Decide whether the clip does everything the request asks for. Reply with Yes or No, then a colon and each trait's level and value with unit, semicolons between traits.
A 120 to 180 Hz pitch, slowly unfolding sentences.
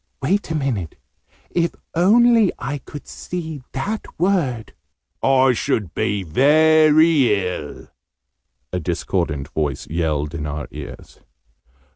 Yes: low, 135 Hz; slow, 115 wpm